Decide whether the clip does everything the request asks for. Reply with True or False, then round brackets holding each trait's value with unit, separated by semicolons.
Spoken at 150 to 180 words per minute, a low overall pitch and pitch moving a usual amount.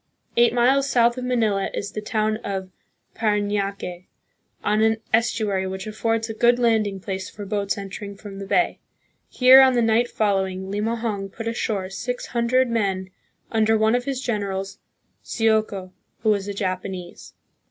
False (155 wpm; 215 Hz; 3.0 semitones)